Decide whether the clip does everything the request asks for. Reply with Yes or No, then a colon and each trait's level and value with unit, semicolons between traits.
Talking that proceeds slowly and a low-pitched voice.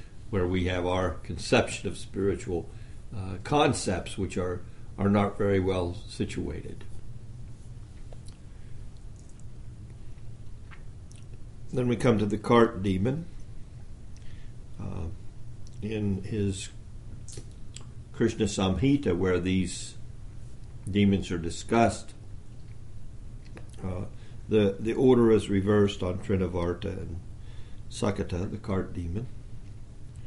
Yes: slow, 90 wpm; low, 110 Hz